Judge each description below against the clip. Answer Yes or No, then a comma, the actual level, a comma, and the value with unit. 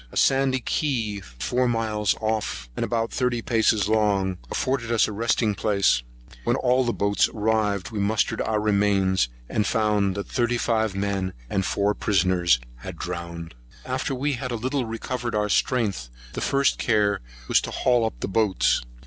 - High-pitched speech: No, low, 110 Hz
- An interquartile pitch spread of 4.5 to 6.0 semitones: No, average, 3.2 semitones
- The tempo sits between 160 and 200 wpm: Yes, average, 170 wpm